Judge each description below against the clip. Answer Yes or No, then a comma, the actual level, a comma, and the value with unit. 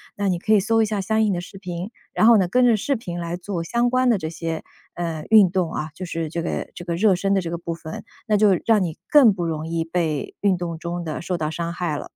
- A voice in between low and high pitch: Yes, medium, 175 Hz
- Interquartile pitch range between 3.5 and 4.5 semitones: Yes, average, 3.9 semitones